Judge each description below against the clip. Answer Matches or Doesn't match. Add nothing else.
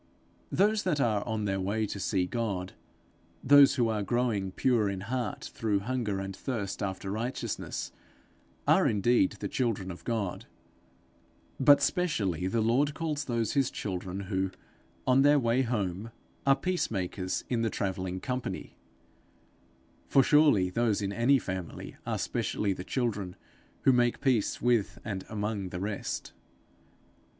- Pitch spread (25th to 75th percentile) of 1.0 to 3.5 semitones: Doesn't match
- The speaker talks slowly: Doesn't match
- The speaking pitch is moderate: Doesn't match